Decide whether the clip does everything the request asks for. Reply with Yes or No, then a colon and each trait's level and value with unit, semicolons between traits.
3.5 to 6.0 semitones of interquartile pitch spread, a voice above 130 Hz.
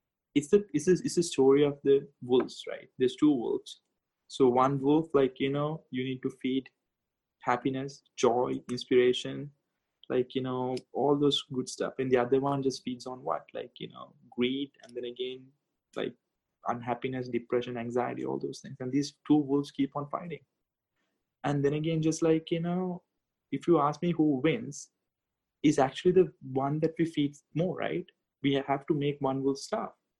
No: average, 3.0 semitones; medium, 140 Hz